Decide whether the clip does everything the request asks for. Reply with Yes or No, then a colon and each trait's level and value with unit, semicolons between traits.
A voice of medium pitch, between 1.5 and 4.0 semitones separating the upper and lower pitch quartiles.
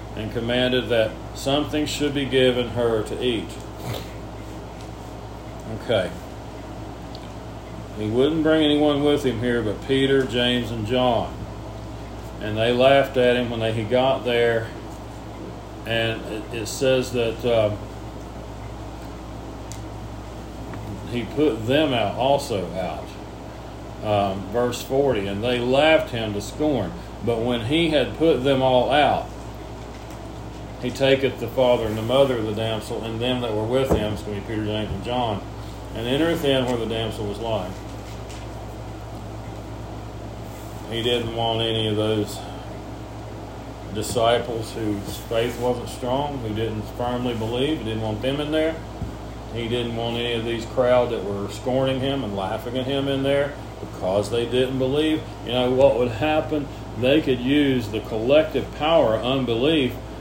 No: low, 115 Hz; average, 3.2 semitones